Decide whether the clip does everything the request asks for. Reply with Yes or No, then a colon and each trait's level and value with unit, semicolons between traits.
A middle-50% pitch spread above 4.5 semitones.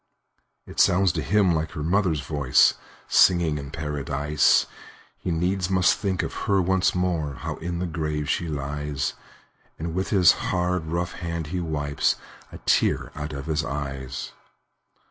No: average, 3.5 semitones